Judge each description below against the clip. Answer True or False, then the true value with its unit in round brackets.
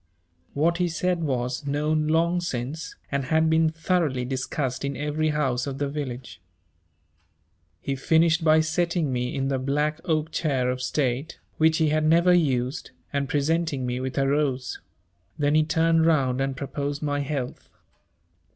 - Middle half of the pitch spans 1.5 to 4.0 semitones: True (3.2 semitones)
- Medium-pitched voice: True (145 Hz)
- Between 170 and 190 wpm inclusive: False (160 wpm)